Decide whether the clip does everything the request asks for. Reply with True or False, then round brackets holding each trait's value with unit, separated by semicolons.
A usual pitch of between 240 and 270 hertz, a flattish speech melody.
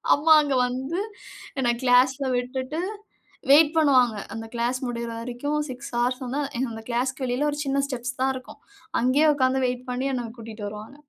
True (255 Hz; 2.1 semitones)